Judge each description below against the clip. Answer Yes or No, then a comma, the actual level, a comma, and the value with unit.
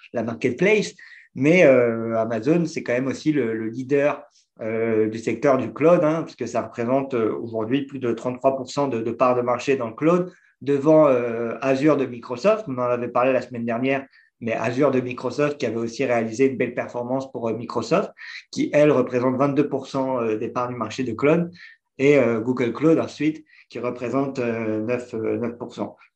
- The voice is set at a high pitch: No, low, 125 Hz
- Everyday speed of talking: Yes, average, 180 wpm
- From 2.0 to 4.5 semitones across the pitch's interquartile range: Yes, average, 3.2 semitones